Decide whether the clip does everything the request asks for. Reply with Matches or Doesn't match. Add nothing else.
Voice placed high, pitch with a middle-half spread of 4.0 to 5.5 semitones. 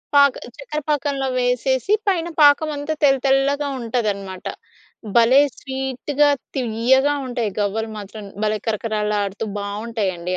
Matches